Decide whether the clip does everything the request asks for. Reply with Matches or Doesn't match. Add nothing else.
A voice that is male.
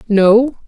Matches